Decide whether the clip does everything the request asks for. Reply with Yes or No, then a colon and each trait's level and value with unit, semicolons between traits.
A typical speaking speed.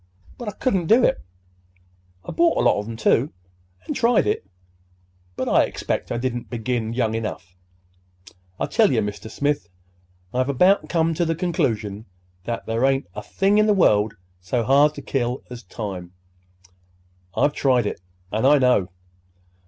Yes: average, 165 wpm